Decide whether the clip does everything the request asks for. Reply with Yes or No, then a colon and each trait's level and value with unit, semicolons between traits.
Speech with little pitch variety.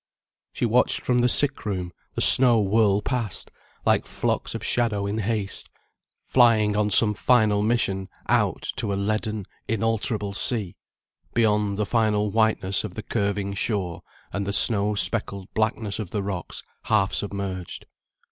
Yes: narrow, 2.2 semitones